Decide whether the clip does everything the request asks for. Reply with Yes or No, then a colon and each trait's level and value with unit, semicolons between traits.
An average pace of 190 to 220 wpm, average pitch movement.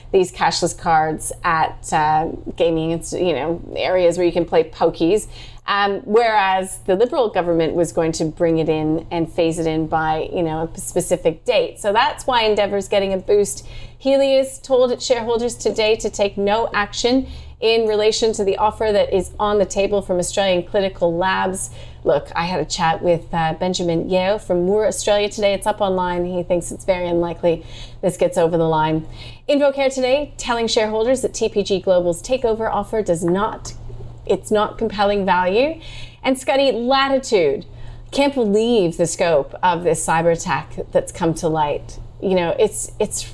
No: average, 170 wpm; average, 4.9 semitones